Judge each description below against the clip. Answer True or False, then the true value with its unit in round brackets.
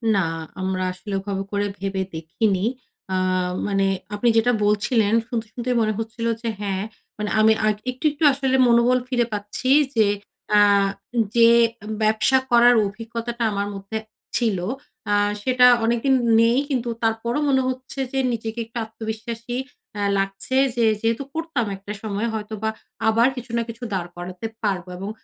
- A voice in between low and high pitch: False (225 Hz)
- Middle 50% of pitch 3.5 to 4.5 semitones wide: False (2.9 semitones)